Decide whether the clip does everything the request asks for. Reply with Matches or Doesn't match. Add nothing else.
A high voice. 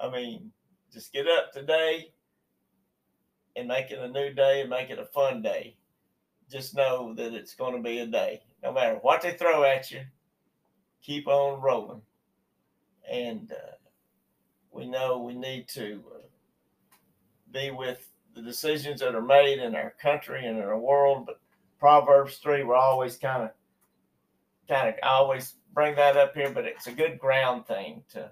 Doesn't match